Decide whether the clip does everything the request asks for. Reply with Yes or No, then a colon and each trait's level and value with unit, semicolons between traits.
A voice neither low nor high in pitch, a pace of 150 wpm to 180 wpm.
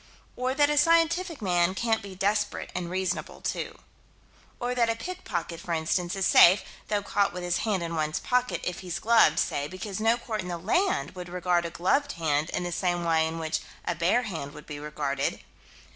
No: medium, 180 Hz; fast, 205 wpm